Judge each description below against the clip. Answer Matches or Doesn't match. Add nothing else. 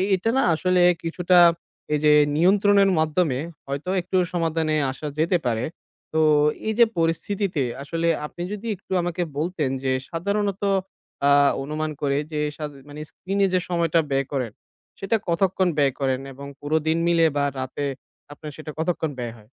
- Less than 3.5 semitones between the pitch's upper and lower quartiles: Doesn't match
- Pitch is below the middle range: Doesn't match